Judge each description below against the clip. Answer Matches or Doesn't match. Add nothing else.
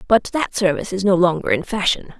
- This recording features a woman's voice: Matches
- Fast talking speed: Matches